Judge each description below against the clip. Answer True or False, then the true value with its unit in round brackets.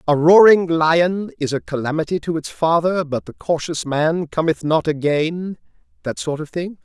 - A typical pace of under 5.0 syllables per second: True (4.6 syllables/s)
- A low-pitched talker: False (155 Hz)